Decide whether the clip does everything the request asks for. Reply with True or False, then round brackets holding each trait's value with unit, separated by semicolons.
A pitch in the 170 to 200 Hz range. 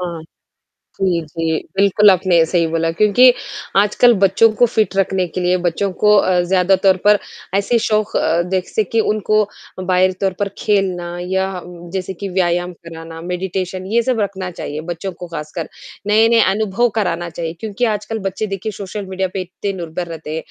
True (190 Hz)